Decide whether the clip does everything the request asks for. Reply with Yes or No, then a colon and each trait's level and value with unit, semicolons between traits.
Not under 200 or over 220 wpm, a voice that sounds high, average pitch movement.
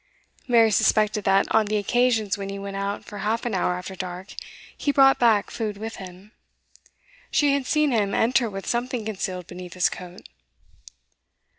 No: average, 170 wpm; high, 210 Hz; average, 3.5 semitones